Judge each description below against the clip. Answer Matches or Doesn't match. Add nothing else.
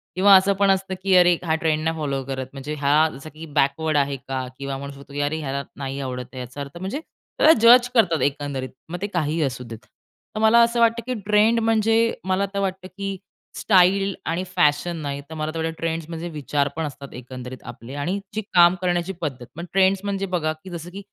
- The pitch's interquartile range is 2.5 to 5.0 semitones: Doesn't match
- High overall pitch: Doesn't match